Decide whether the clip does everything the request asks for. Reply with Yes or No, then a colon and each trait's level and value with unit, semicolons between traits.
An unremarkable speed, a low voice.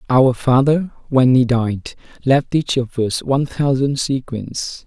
Yes: average, 150 wpm; low, 130 Hz